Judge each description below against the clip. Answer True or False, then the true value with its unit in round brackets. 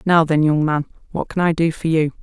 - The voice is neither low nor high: True (160 Hz)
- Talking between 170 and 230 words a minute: False (270 wpm)